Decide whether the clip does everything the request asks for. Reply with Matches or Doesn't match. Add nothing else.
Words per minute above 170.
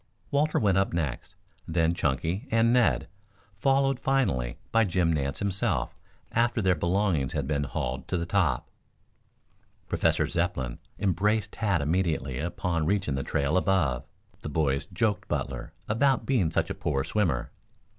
Doesn't match